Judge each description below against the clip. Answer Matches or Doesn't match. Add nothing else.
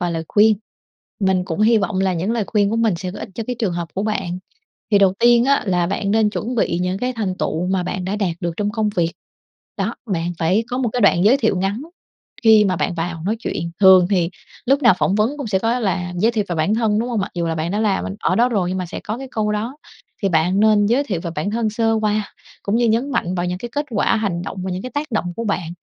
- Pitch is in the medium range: Doesn't match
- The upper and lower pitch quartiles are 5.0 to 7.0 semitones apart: Doesn't match